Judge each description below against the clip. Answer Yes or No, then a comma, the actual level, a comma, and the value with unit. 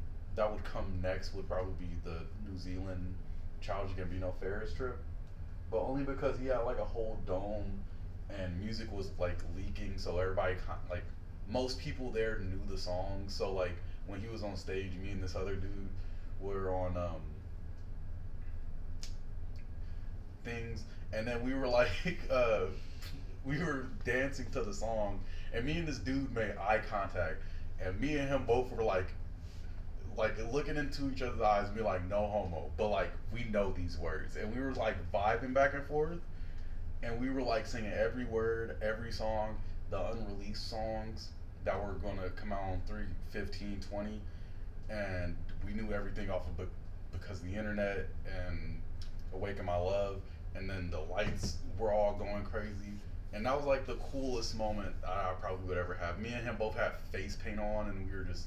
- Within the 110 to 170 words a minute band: No, average, 180 wpm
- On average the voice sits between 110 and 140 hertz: No, very low, 95 Hz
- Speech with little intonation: No, average, 3.2 semitones